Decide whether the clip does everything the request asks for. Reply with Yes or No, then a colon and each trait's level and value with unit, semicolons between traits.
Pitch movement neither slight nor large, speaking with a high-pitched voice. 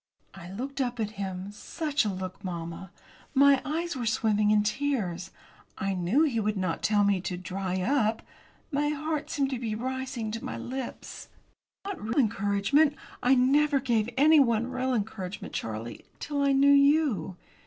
No: wide, 6.0 semitones; high, 230 Hz